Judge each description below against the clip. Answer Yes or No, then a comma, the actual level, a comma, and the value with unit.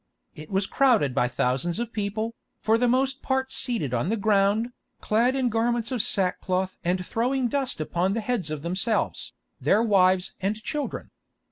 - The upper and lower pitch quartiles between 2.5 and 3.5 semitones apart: No, average, 4.7 semitones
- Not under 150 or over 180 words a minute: Yes, average, 170 wpm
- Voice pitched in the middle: No, high, 215 Hz